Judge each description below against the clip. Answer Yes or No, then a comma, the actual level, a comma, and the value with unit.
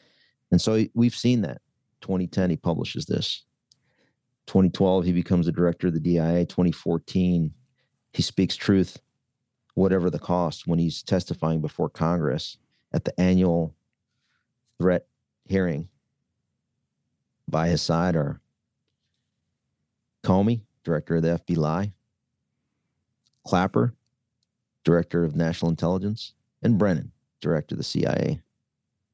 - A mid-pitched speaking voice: No, very low, 90 Hz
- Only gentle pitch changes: No, average, 4.6 semitones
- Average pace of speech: No, slow, 110 wpm